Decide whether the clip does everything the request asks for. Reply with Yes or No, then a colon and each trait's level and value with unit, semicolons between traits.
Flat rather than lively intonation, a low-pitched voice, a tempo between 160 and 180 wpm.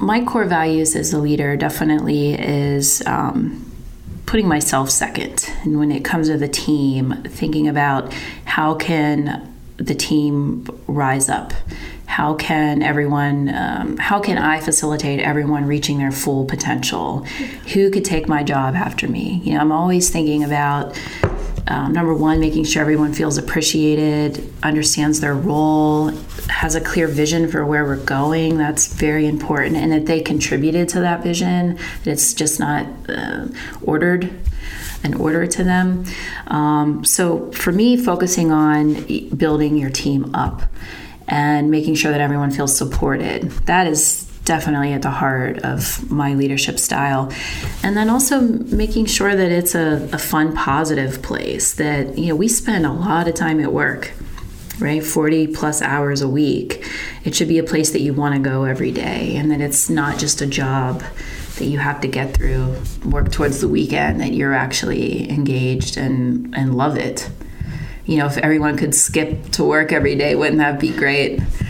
No: narrow, 2.1 semitones; medium, 150 Hz; average, 165 wpm